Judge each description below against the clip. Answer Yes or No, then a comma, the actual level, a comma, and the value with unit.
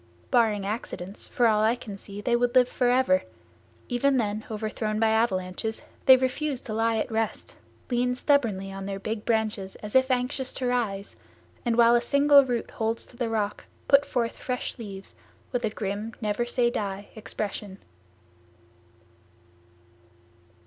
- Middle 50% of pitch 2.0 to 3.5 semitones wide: Yes, average, 2.9 semitones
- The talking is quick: No, average, 155 wpm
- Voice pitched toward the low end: No, high, 225 Hz